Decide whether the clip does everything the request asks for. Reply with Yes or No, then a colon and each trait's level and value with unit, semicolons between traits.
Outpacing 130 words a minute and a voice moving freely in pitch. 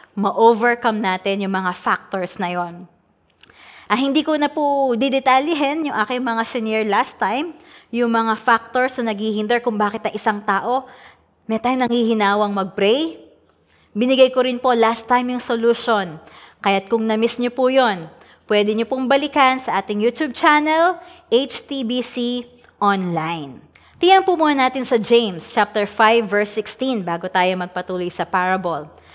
No: average, 150 wpm; average, 4.4 semitones